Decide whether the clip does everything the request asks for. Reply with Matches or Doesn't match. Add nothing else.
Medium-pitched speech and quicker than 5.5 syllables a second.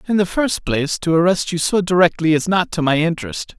Matches